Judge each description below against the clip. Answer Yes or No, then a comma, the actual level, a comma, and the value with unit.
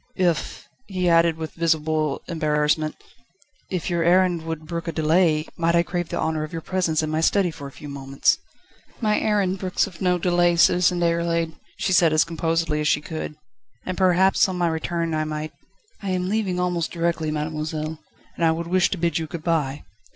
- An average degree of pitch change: No, narrow, 2.3 semitones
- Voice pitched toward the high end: No, medium, 165 Hz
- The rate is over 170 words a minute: Yes, average, 200 wpm